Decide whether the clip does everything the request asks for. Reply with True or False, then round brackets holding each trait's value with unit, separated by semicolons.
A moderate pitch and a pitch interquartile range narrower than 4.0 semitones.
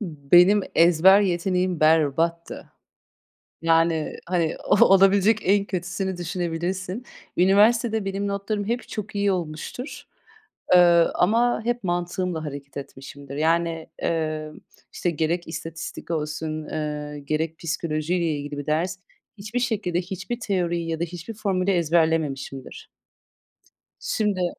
True (175 Hz; 3.6 semitones)